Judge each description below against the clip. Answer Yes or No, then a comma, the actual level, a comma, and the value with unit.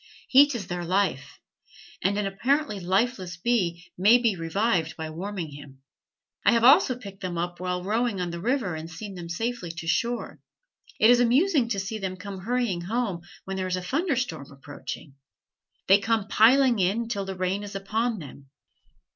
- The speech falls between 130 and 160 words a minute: No, average, 180 wpm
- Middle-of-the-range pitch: No, high, 195 Hz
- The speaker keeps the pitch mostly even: No, average, 5.1 semitones